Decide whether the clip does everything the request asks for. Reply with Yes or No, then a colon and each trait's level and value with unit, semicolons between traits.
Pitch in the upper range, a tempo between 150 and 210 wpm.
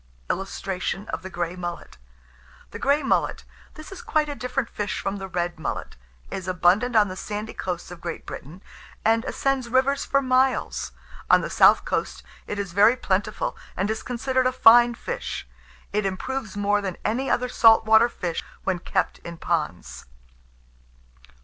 Yes: high, 210 Hz; average, 160 wpm